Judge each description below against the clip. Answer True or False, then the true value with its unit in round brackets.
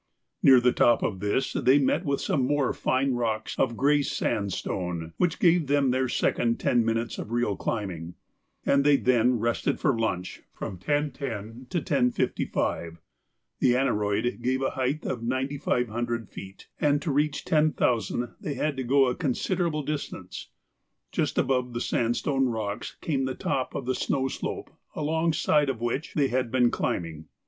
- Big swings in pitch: False (3.7 semitones)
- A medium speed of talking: True (160 wpm)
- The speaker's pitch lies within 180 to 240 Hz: False (125 Hz)